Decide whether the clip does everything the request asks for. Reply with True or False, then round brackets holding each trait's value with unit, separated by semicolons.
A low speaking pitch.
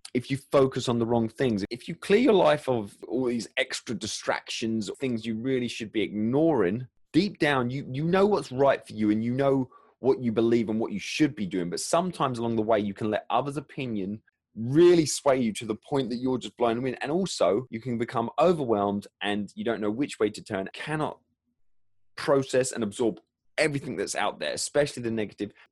True (120 Hz)